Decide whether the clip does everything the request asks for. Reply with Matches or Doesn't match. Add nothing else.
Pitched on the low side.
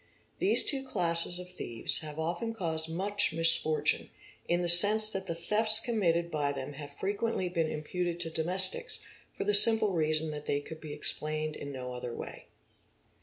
Doesn't match